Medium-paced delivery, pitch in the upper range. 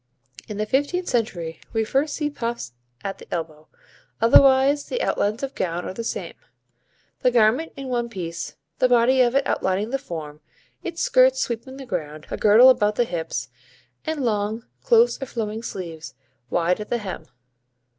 Yes: average, 170 wpm; high, 230 Hz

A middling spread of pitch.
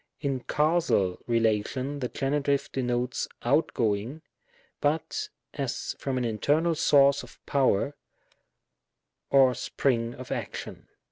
Yes: average, 3.2 semitones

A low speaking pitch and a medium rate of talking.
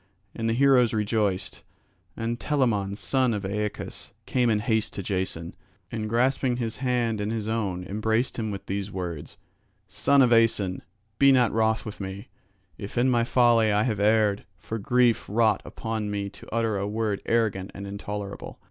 Yes: low, 110 Hz; average, 170 wpm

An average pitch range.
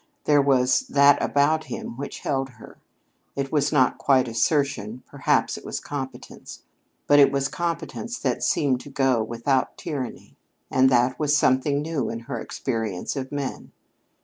No: narrow, 2.2 semitones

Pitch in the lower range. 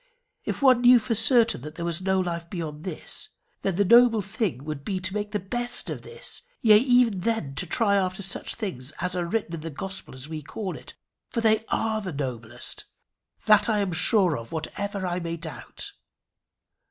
No: high, 190 Hz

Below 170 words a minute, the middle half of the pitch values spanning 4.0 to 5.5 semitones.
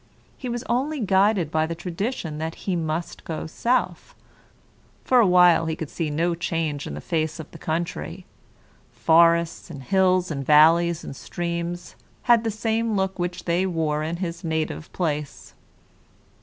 No: average, 160 wpm; average, 3.1 semitones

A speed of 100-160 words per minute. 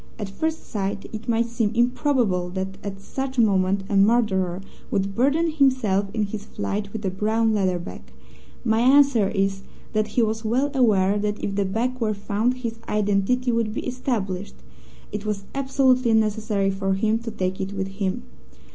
No: average, 175 wpm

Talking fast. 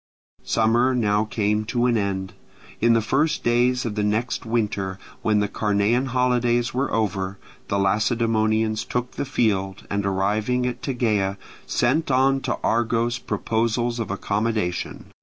No: average, 140 wpm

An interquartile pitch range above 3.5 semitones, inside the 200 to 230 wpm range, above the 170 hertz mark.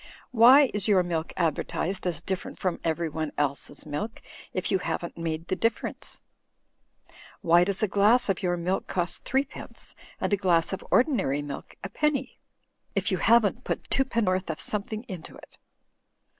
No: average, 4.8 semitones; average, 155 wpm; medium, 185 Hz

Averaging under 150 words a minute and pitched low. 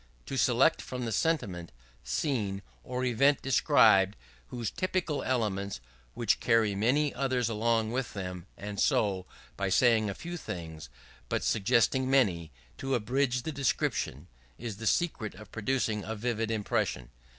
Yes: average, 140 wpm; low, 115 Hz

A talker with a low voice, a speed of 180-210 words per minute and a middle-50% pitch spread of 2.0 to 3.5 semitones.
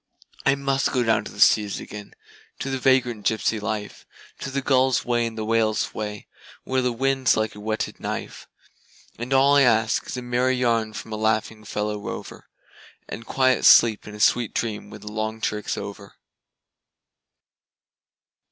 No: low, 115 Hz; average, 170 wpm; average, 3.2 semitones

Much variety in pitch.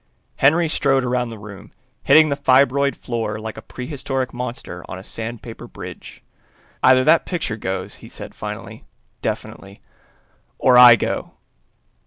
No: average, 3.6 semitones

